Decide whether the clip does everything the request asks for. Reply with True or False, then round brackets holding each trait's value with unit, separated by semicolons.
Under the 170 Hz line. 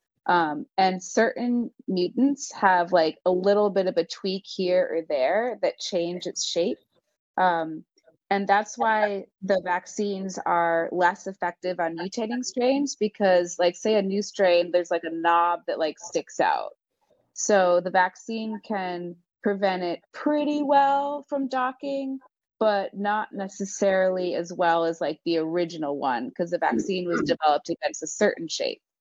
False (190 Hz)